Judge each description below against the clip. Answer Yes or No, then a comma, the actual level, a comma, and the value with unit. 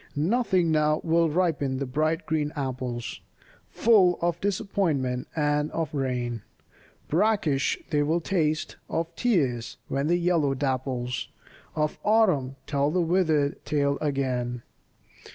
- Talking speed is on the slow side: Yes, slow, 120 wpm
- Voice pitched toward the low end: No, medium, 150 Hz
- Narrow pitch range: No, average, 4.1 semitones